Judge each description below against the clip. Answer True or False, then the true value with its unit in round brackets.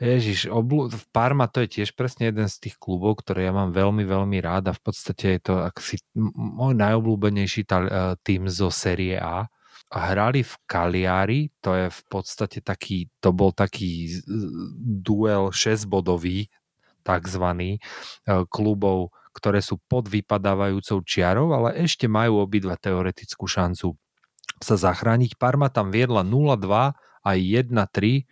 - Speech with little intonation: False (3.4 semitones)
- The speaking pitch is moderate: False (100 Hz)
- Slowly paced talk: False (140 wpm)